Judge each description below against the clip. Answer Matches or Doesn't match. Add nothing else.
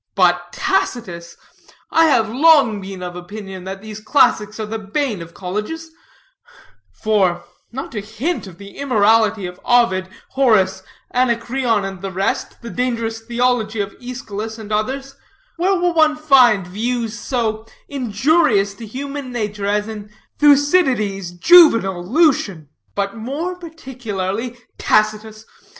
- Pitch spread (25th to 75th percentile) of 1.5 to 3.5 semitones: Doesn't match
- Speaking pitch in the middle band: Doesn't match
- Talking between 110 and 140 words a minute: Matches